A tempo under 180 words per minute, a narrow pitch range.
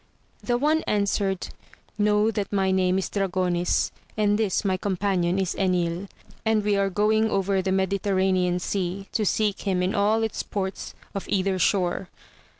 Yes: average, 155 wpm; narrow, 1.8 semitones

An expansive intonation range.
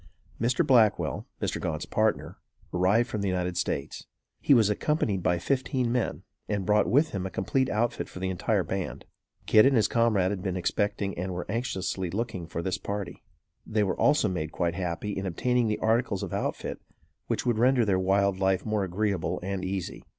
No: average, 3.6 semitones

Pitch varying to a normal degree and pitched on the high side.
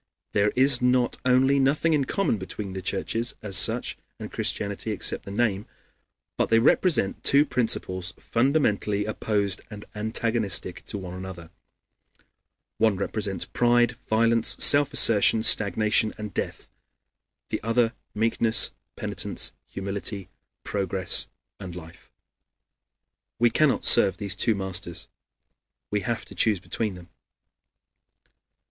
No: average, 3.5 semitones; low, 105 Hz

